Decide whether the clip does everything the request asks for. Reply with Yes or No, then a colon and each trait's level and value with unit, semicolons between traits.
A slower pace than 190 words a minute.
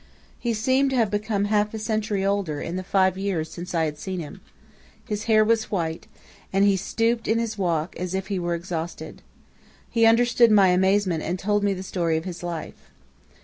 No: average, 200 wpm